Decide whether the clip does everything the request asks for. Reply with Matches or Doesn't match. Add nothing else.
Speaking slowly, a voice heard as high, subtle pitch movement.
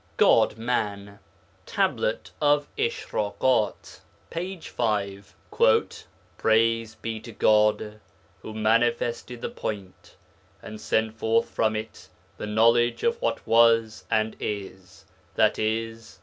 Doesn't match